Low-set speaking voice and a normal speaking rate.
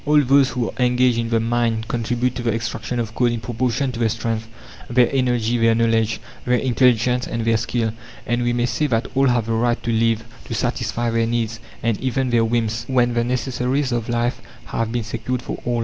No: low, 120 Hz; fast, 215 wpm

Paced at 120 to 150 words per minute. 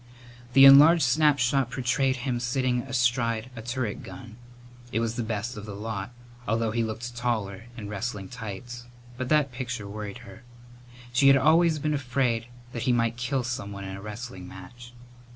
No: average, 170 wpm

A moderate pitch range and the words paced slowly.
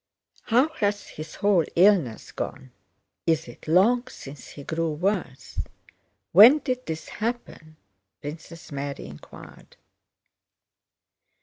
No: wide, 6.0 semitones; slow, 105 wpm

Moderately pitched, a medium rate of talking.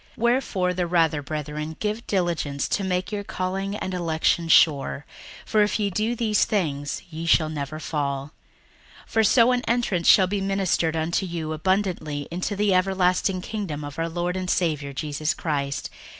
Yes: medium, 175 Hz; average, 170 wpm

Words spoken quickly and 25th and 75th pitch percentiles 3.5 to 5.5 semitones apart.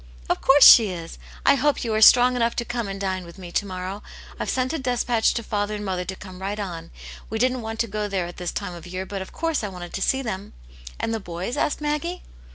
Yes: fast, 275 wpm; average, 4.6 semitones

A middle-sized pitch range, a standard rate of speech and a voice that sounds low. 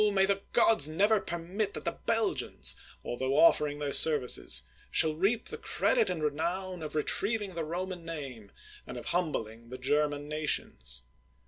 No: average, 4.8 semitones; average, 150 wpm; medium, 160 Hz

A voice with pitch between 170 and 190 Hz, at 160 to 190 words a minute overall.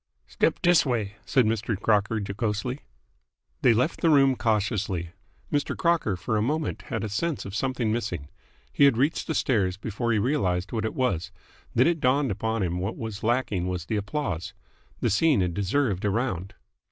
No: low, 110 Hz; average, 185 wpm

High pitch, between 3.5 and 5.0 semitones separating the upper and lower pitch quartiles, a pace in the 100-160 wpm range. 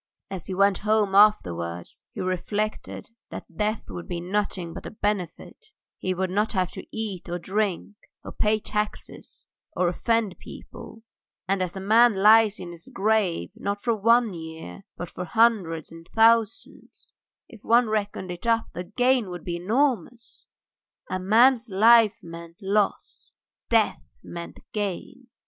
Yes: high, 205 Hz; average, 3.8 semitones; average, 150 wpm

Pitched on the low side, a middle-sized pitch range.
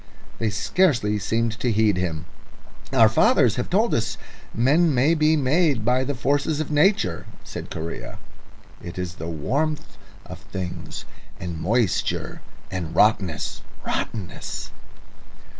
No: low, 115 Hz; wide, 8.0 semitones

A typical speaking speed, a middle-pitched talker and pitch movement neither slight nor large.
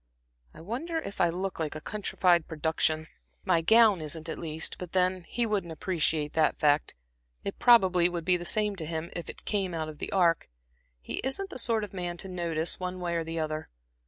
No: fast, 210 wpm; medium, 175 Hz; average, 3.3 semitones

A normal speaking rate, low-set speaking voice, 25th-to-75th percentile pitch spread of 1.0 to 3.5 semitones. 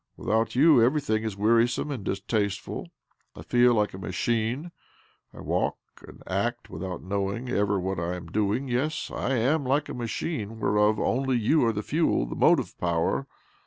No: average, 165 wpm; low, 110 Hz; average, 4.2 semitones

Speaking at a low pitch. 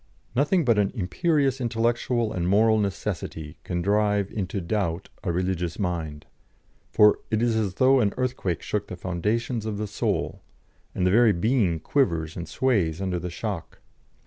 Yes: low, 100 Hz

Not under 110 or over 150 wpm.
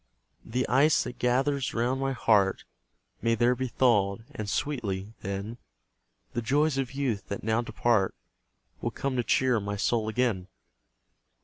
Yes: average, 145 wpm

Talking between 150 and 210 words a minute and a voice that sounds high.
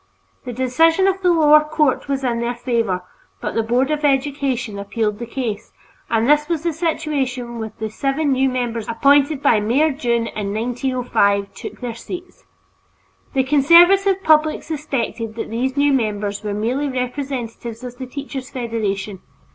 Yes: average, 160 wpm; very high, 255 Hz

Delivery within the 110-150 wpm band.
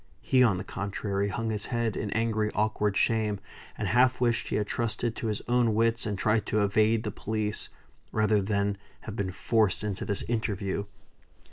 No: average, 180 wpm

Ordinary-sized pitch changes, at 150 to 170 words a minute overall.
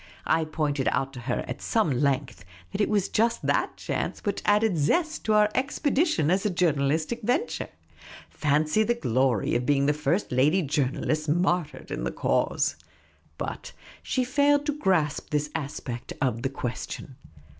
No: wide, 7.4 semitones; average, 160 wpm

